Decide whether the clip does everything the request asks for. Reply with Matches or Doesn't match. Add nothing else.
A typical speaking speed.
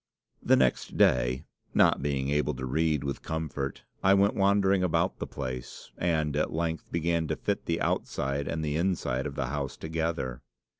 Matches